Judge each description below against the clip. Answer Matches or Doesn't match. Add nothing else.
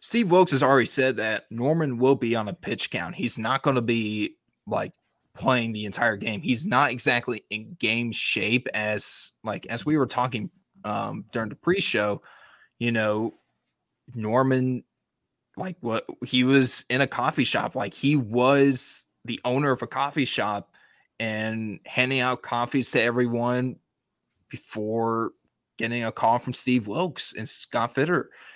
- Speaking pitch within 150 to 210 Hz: Doesn't match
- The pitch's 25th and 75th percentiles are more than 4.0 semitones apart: Doesn't match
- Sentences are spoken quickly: Doesn't match